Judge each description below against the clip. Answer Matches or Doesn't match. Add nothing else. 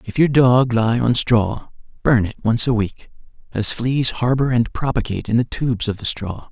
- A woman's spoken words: Doesn't match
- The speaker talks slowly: Doesn't match